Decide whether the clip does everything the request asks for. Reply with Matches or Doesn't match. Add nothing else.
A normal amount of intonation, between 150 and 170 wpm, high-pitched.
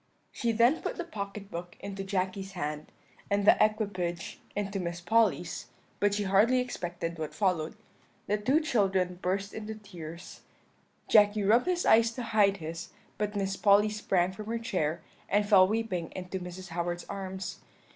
Matches